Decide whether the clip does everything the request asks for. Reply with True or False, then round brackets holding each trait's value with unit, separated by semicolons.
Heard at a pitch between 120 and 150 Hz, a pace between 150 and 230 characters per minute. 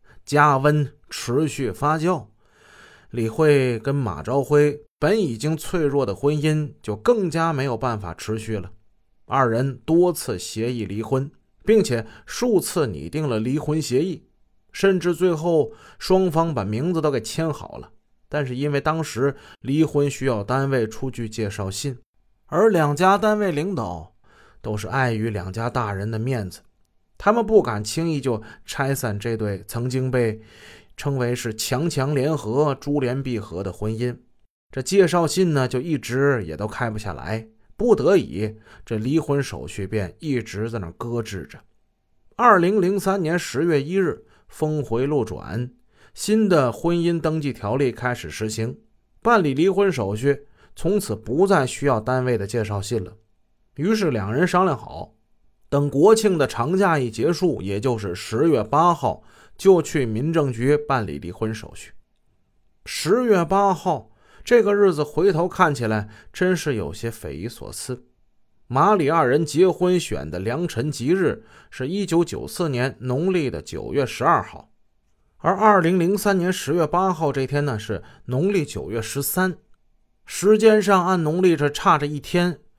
True (135 Hz; 225 characters per minute)